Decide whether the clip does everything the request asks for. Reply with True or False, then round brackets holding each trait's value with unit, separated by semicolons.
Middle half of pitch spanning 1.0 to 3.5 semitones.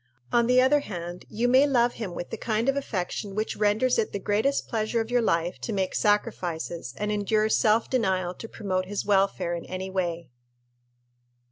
False (3.9 semitones)